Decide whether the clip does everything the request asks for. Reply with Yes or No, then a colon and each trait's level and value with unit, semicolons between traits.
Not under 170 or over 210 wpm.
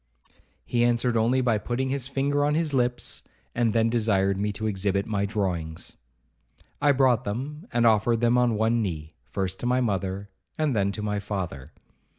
Yes: average, 175 wpm